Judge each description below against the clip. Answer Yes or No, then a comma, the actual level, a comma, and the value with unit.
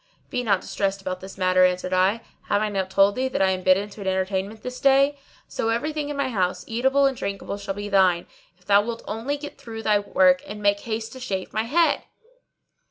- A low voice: No, high, 205 Hz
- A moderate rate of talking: No, fast, 230 wpm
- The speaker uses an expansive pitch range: No, average, 4.2 semitones